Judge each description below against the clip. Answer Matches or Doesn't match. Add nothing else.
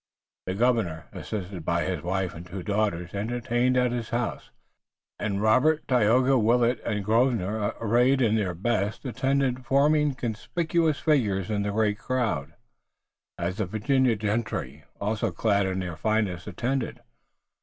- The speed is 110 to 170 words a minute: Matches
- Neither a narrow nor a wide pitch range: Matches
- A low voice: Matches